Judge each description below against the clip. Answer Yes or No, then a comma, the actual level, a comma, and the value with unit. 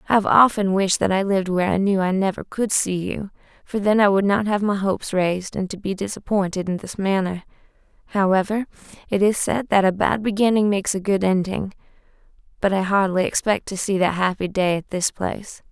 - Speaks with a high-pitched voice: Yes, high, 195 Hz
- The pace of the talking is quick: Yes, fast, 210 wpm